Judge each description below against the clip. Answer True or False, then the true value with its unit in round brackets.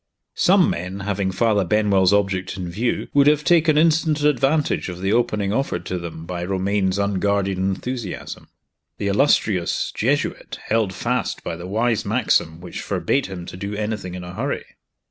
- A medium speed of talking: True (165 wpm)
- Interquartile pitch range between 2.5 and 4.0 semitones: False (4.4 semitones)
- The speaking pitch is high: False (100 Hz)